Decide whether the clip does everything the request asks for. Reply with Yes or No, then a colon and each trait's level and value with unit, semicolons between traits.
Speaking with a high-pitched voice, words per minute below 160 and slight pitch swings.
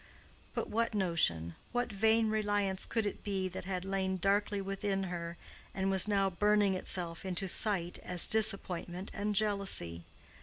Yes: high, 195 Hz; average, 150 wpm; narrow, 2.3 semitones